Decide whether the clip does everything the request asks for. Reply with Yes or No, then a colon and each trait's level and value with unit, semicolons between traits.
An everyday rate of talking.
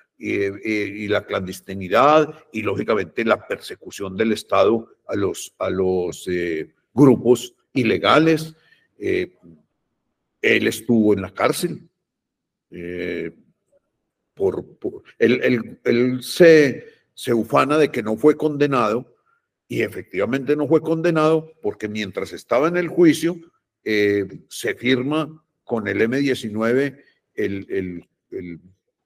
No: slow, 115 wpm